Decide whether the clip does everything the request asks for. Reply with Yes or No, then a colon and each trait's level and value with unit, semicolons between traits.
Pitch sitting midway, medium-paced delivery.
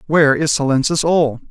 Yes: medium, 150 Hz; average, 160 wpm